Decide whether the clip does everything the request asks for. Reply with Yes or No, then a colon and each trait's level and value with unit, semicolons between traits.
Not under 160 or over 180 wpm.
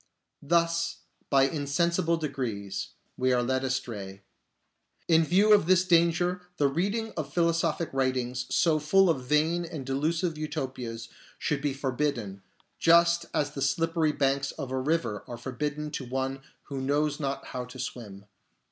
No: average, 150 wpm